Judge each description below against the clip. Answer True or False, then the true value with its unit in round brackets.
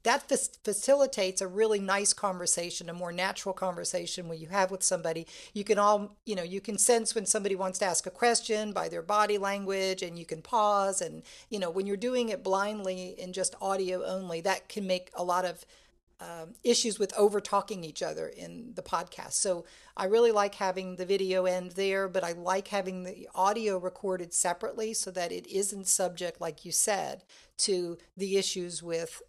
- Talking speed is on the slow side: False (195 wpm)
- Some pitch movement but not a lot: False (2.3 semitones)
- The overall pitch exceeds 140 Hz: True (190 Hz)